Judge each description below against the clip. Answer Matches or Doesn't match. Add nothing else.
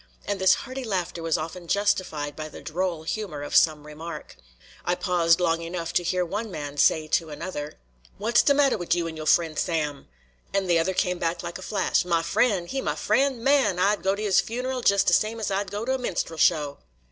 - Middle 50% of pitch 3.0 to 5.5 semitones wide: Matches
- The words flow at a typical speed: Doesn't match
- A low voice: Doesn't match